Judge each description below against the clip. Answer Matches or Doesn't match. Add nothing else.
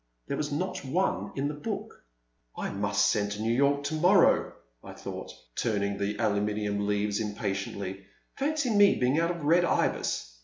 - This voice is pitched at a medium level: Doesn't match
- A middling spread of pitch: Doesn't match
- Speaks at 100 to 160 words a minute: Doesn't match